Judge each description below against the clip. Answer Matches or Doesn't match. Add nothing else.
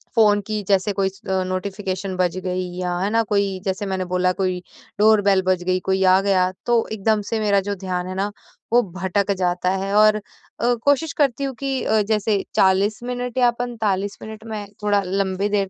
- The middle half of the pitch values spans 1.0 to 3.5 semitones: Matches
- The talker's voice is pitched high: Matches